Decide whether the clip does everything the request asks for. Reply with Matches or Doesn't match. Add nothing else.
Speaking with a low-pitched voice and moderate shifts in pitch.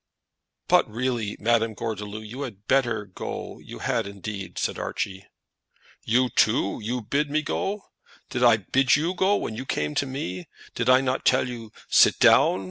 Matches